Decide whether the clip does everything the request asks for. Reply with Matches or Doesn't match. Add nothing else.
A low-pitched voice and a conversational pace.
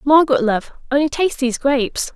Doesn't match